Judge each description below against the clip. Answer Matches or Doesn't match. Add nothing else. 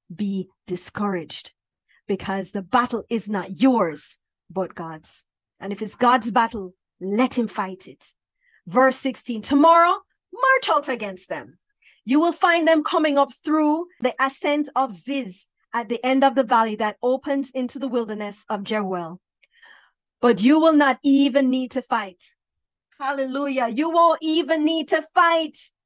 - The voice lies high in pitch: Matches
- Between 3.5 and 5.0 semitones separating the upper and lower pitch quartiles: Doesn't match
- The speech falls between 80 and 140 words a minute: Doesn't match